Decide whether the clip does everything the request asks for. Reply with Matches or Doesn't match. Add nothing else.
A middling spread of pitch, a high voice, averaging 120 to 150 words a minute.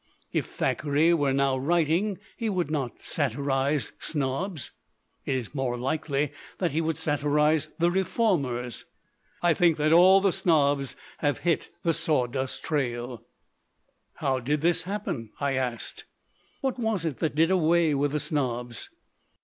Doesn't match